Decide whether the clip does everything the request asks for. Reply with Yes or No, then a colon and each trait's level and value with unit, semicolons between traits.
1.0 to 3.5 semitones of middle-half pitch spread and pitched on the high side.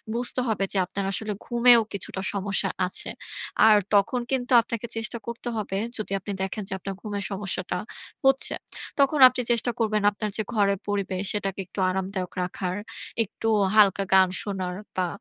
Yes: average, 3.0 semitones; high, 205 Hz